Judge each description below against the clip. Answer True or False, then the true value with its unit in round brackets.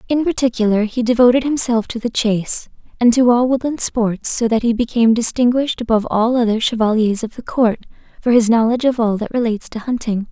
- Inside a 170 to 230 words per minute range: True (200 wpm)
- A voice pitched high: True (235 Hz)